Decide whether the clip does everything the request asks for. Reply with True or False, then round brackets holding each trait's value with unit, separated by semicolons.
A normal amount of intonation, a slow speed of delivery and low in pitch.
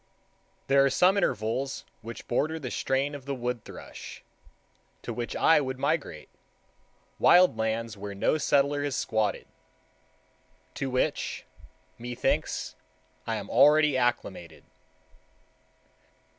True (4.1 semitones; 110 wpm; 130 Hz)